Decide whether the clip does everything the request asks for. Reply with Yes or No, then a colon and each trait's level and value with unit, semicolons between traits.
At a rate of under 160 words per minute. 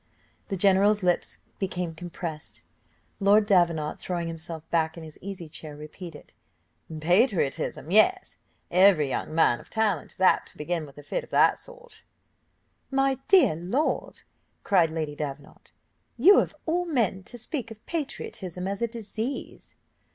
Yes: average, 145 wpm